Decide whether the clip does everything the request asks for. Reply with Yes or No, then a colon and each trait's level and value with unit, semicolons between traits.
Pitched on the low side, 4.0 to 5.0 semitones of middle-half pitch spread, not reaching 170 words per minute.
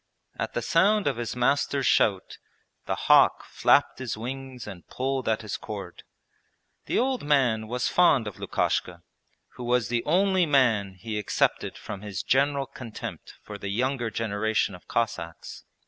Yes: low, 120 Hz; average, 4.4 semitones; average, 155 wpm